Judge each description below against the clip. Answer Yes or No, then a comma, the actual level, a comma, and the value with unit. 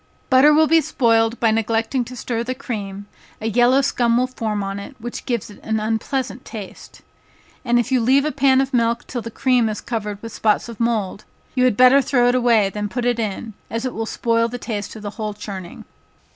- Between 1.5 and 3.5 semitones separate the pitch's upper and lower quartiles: Yes, average, 2.7 semitones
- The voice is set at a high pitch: Yes, high, 230 Hz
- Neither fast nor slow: No, fast, 220 wpm